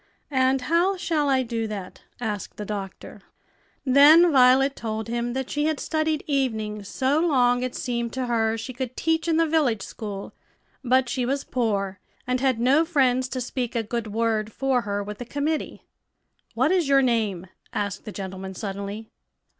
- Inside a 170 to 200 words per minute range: Yes, average, 175 wpm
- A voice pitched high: Yes, very high, 250 Hz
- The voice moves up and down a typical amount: Yes, average, 4.1 semitones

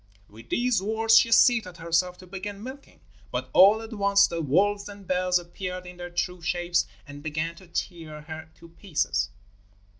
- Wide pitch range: No, average, 3.5 semitones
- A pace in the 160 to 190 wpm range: Yes, average, 175 wpm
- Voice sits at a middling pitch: Yes, medium, 180 Hz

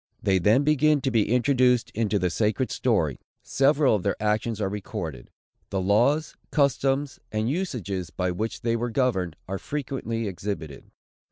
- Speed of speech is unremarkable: Yes, average, 155 wpm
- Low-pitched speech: Yes, low, 115 Hz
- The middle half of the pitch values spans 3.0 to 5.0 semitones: No, wide, 5.4 semitones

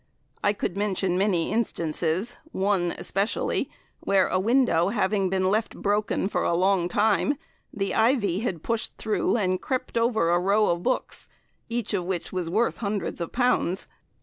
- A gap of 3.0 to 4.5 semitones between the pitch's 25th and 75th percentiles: Yes, average, 3.3 semitones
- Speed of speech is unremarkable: Yes, average, 160 wpm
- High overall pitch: Yes, high, 195 Hz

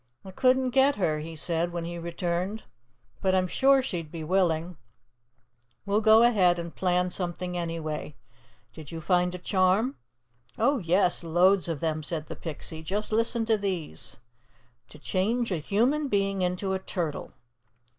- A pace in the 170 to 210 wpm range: No, average, 155 wpm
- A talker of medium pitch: Yes, medium, 180 Hz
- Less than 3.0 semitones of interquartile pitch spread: No, average, 3.6 semitones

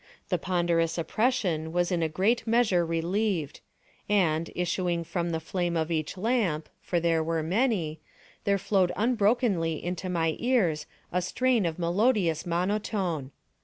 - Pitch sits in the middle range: Yes, medium, 175 Hz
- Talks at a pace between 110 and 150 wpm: Yes, average, 140 wpm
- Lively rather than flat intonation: No, average, 3.9 semitones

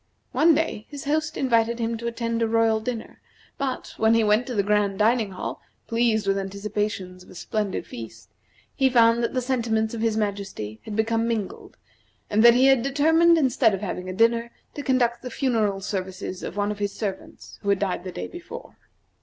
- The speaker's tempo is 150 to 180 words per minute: No, average, 200 wpm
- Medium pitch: No, high, 225 Hz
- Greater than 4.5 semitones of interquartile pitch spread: No, average, 3.2 semitones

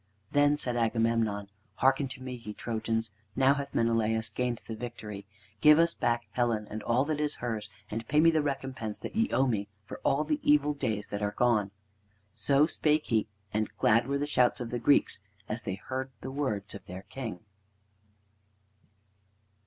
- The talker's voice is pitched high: No, low, 120 Hz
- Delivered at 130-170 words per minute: No, average, 180 wpm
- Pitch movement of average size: Yes, average, 4.3 semitones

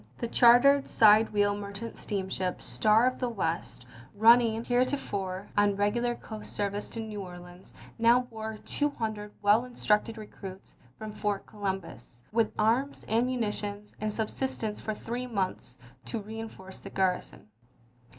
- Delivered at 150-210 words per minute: No, average, 140 wpm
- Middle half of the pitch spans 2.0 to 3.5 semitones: Yes, narrow, 2.6 semitones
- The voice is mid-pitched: No, high, 215 Hz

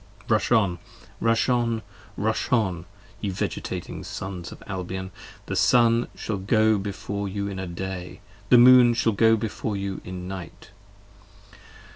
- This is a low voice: Yes, low, 100 Hz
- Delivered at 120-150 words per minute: Yes, average, 140 wpm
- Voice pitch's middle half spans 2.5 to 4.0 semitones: Yes, average, 3.4 semitones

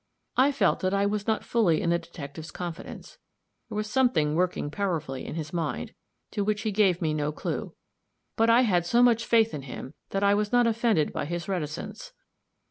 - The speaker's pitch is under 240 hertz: Yes, high, 190 Hz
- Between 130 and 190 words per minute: No, average, 200 wpm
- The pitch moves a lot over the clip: Yes, wide, 5.8 semitones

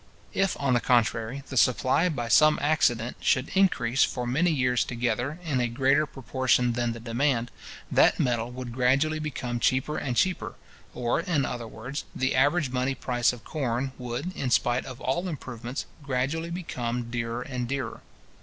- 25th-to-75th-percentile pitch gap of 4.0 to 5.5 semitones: No, average, 2.8 semitones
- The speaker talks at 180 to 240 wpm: No, average, 165 wpm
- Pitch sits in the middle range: No, low, 125 Hz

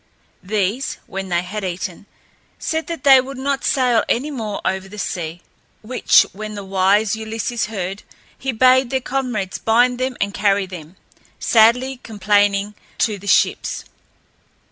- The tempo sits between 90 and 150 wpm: Yes, average, 145 wpm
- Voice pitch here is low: No, high, 215 Hz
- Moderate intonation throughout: Yes, average, 4.5 semitones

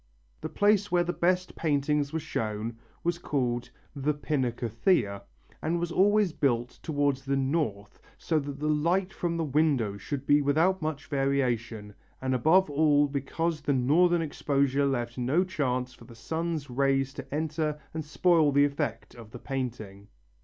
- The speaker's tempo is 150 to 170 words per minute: Yes, average, 160 wpm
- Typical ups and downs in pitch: Yes, average, 4.0 semitones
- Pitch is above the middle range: No, medium, 145 Hz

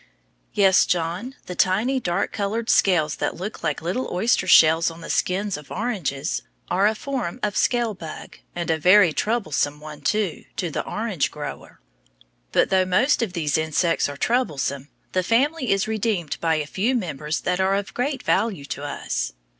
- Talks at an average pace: Yes, average, 175 wpm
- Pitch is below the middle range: No, medium, 185 Hz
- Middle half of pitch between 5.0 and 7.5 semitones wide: Yes, wide, 5.6 semitones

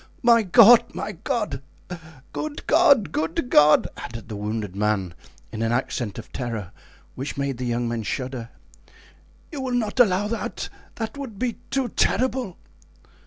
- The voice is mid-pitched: Yes, medium, 155 Hz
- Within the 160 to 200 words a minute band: No, average, 150 wpm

